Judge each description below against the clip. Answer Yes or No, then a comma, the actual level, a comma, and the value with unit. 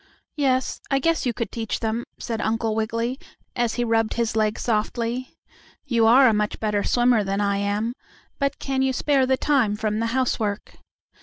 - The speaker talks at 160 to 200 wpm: Yes, average, 180 wpm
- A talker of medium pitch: No, high, 230 Hz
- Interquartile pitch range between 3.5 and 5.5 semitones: No, average, 3.0 semitones